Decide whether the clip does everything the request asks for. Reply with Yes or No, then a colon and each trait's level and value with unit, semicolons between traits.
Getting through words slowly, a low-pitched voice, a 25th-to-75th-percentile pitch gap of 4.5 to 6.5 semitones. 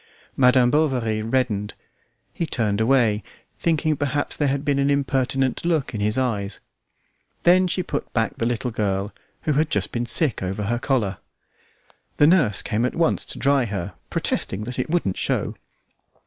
No: average, 165 wpm; low, 125 Hz; average, 5.1 semitones